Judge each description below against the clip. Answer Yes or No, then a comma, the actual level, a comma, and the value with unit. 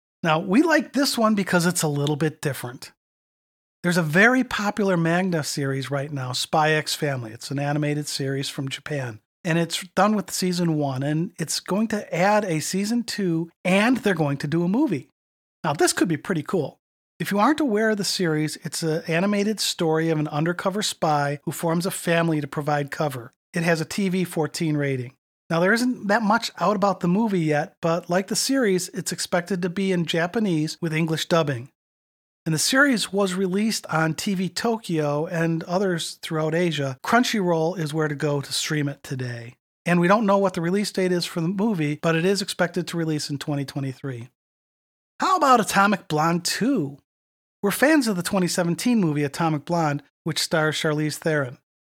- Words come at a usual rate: Yes, average, 190 wpm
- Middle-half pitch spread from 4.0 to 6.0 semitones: Yes, average, 4.7 semitones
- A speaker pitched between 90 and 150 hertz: No, medium, 170 Hz